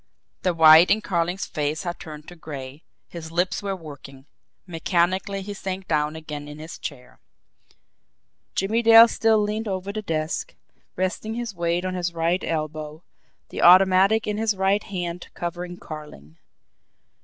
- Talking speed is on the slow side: No, average, 150 wpm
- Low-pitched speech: No, medium, 175 Hz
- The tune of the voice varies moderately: Yes, average, 3.8 semitones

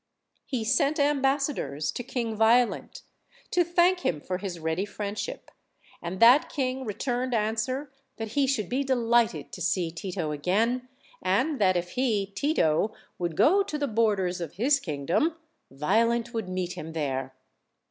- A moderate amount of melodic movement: No, wide, 6.5 semitones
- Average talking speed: Yes, average, 155 wpm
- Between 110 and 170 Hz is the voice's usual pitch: No, high, 220 Hz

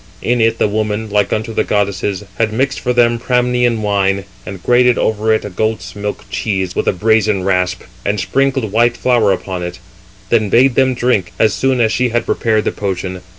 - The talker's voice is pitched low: Yes, low, 110 Hz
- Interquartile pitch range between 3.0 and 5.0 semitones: Yes, average, 3.5 semitones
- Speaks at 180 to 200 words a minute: Yes, average, 195 wpm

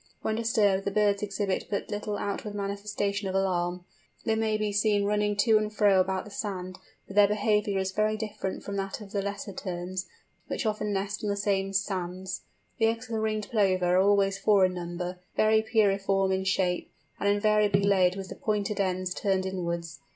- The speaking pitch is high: Yes, high, 200 Hz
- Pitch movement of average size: No, narrow, 1.8 semitones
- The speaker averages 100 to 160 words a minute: No, average, 195 wpm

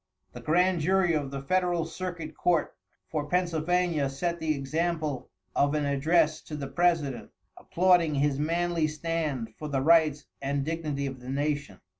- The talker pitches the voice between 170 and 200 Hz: No, medium, 155 Hz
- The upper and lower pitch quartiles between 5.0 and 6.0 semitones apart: No, average, 3.3 semitones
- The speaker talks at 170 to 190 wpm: No, average, 155 wpm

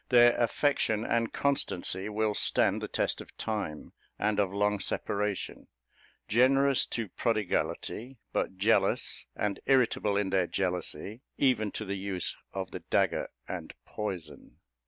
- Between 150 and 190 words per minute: No, slow, 135 wpm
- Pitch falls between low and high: No, low, 105 Hz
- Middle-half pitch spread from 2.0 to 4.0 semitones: Yes, average, 3.3 semitones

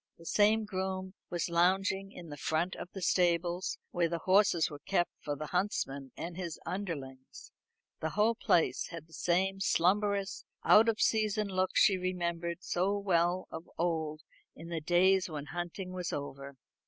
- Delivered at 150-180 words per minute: Yes, average, 160 wpm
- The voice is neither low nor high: Yes, medium, 175 Hz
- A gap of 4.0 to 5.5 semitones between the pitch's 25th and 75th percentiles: No, narrow, 2.5 semitones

